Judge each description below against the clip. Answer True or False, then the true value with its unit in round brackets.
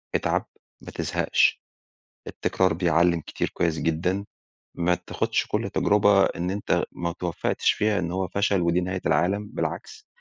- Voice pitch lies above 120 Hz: False (90 Hz)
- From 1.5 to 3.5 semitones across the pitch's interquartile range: True (2.6 semitones)